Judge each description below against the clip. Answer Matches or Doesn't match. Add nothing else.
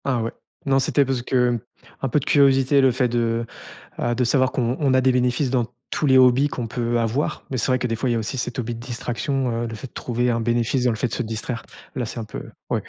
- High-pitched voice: Doesn't match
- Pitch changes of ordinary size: Doesn't match